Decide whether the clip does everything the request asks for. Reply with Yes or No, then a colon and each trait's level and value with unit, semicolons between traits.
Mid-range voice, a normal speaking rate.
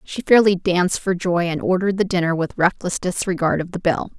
No: medium, 180 Hz; fast, 215 wpm